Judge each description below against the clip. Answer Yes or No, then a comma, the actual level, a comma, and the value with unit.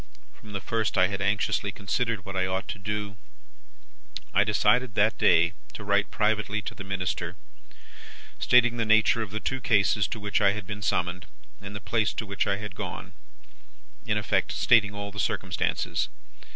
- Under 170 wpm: No, average, 180 wpm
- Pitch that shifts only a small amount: Yes, narrow, 1.6 semitones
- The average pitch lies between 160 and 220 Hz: No, low, 105 Hz